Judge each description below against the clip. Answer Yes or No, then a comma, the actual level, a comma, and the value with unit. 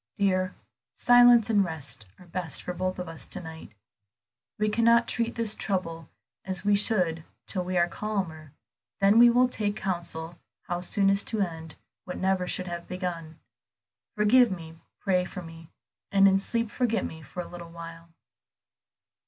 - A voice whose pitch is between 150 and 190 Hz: Yes, medium, 185 Hz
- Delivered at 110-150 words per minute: No, average, 165 wpm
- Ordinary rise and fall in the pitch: Yes, average, 3.8 semitones